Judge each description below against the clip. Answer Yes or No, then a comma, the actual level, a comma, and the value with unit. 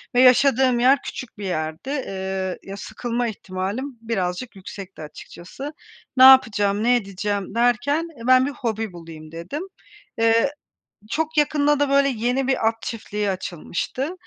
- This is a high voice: Yes, high, 230 Hz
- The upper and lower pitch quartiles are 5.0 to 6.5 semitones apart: Yes, wide, 5.5 semitones